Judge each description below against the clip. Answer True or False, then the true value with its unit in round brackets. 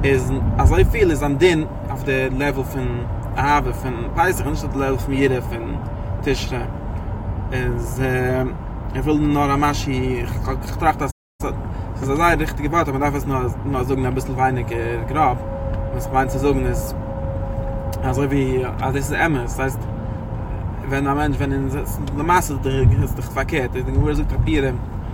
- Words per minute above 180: False (165 wpm)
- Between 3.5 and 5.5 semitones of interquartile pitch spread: True (3.9 semitones)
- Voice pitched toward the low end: True (130 Hz)